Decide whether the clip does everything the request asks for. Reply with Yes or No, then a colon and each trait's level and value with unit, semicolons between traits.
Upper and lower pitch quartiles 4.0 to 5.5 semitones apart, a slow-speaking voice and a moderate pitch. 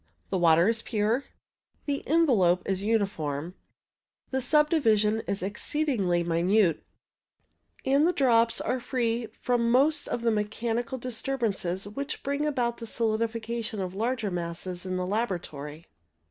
No: average, 5.1 semitones; slow, 130 wpm; high, 225 Hz